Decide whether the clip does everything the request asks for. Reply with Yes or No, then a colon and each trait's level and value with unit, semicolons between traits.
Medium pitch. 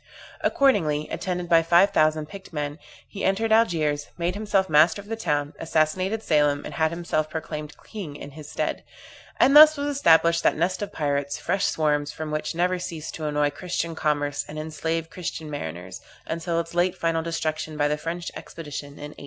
Yes: medium, 160 Hz